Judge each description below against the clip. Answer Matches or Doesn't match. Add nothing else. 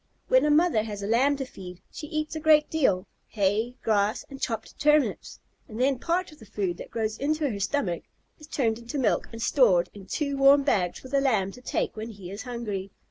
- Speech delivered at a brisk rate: Matches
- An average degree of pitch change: Doesn't match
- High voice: Matches